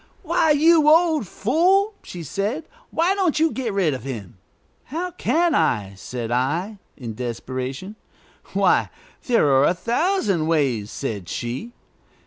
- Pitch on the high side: Yes, high, 195 Hz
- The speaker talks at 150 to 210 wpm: No, slow, 135 wpm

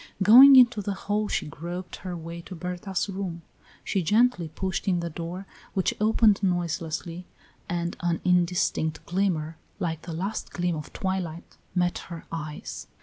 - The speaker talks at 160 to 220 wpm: No, average, 150 wpm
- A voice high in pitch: No, medium, 180 Hz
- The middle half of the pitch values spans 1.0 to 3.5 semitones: Yes, narrow, 2.6 semitones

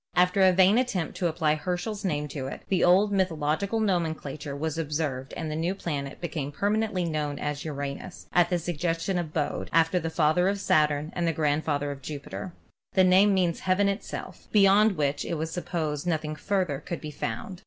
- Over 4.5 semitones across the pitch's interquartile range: No, average, 3.8 semitones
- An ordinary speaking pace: Yes, average, 195 wpm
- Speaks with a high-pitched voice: No, medium, 165 Hz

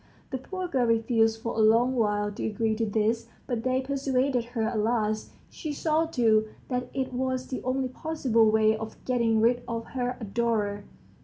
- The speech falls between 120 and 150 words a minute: No, average, 180 wpm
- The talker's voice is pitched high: Yes, high, 235 Hz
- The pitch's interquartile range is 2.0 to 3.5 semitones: Yes, average, 2.7 semitones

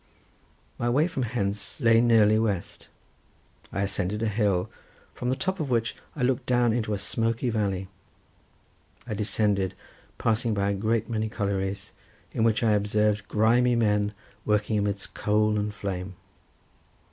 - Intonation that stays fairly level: Yes, narrow, 2.2 semitones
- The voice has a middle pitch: No, low, 105 Hz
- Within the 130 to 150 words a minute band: Yes, average, 145 wpm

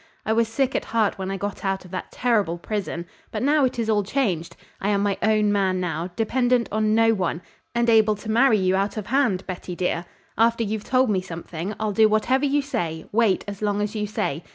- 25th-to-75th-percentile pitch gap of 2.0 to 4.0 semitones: Yes, average, 3.4 semitones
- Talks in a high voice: Yes, high, 210 Hz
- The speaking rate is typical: No, fast, 225 wpm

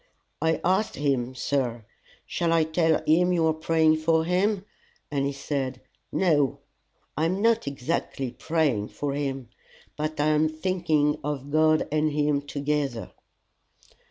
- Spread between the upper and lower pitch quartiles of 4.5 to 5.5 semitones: No, narrow, 2.6 semitones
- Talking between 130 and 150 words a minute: Yes, average, 140 wpm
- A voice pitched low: No, medium, 155 Hz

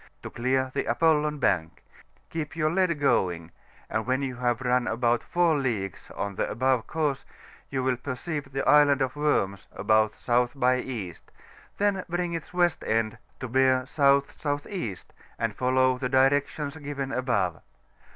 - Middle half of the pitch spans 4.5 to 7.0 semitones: No, average, 3.5 semitones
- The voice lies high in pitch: No, low, 130 Hz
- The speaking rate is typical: Yes, average, 150 wpm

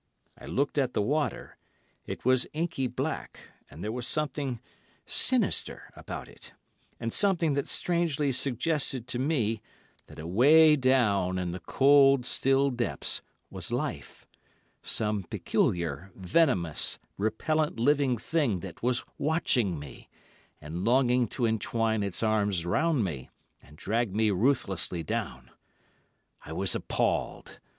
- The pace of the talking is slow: Yes, slow, 125 wpm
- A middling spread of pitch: No, wide, 6.2 semitones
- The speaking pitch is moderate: No, low, 120 Hz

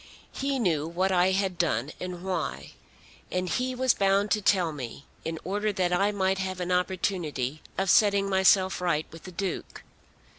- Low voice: No, medium, 185 Hz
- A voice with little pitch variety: Yes, narrow, 2.2 semitones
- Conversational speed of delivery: Yes, average, 175 wpm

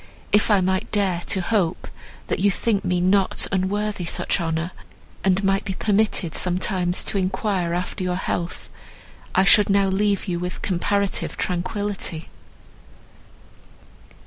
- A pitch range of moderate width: No, narrow, 2.1 semitones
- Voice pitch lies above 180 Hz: Yes, high, 190 Hz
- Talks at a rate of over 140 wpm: No, slow, 135 wpm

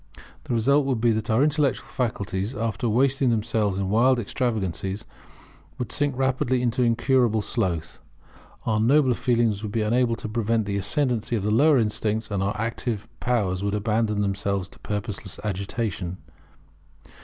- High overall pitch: No, low, 110 Hz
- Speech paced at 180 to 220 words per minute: No, average, 155 wpm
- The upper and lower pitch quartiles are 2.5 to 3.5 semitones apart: Yes, average, 3.2 semitones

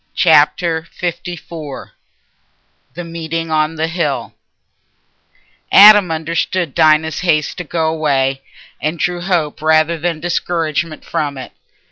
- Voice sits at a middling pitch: Yes, medium, 160 Hz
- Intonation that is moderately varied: No, narrow, 1.9 semitones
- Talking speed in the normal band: No, slow, 110 wpm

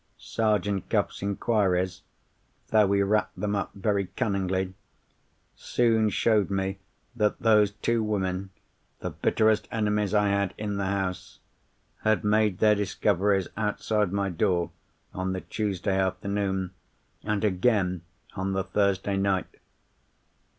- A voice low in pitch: Yes, low, 100 Hz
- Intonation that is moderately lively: No, narrow, 1.8 semitones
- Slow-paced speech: Yes, slow, 115 wpm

